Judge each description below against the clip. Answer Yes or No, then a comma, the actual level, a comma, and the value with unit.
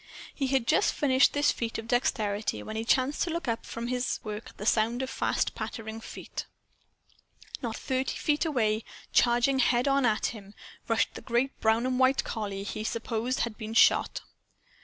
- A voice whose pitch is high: Yes, high, 235 Hz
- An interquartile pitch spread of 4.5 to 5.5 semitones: No, average, 2.9 semitones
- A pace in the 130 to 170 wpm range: No, average, 180 wpm